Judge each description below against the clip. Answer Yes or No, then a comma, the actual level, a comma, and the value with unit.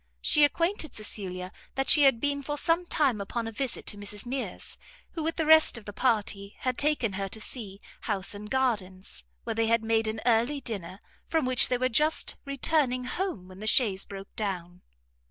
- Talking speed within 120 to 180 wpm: No, average, 195 wpm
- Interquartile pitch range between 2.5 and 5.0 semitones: No, wide, 5.4 semitones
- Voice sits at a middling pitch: No, high, 230 Hz